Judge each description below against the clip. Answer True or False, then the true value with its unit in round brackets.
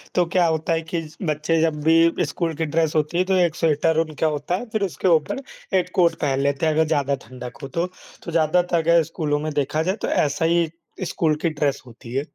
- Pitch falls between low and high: True (160 Hz)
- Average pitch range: False (2.2 semitones)